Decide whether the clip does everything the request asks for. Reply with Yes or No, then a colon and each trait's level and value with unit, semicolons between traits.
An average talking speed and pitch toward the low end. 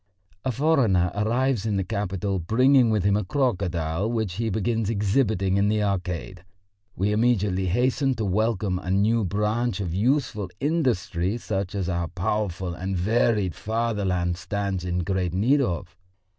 Yes: average, 150 wpm; low, 100 Hz